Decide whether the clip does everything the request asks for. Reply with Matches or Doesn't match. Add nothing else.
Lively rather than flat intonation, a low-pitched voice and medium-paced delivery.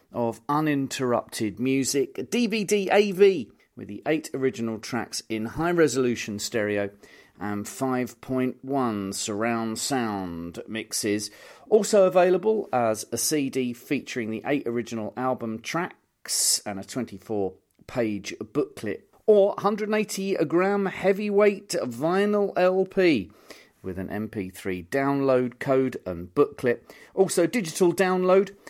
Doesn't match